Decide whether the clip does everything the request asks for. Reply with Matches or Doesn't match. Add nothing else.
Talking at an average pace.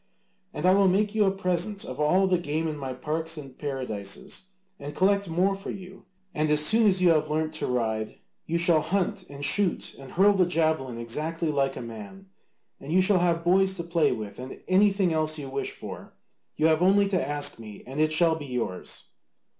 Doesn't match